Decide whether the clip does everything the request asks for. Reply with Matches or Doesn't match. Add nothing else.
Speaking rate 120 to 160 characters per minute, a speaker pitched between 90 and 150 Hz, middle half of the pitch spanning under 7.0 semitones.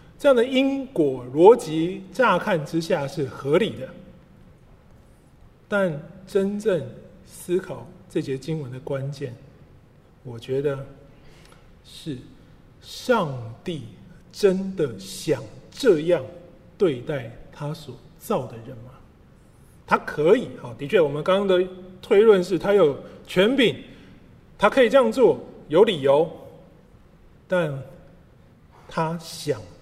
Doesn't match